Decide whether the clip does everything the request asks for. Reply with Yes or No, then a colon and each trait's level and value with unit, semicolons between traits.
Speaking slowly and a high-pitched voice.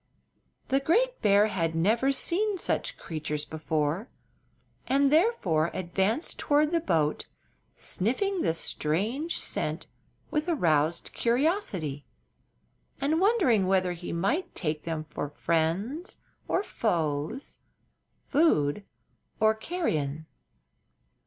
Yes: slow, 100 wpm; high, 200 Hz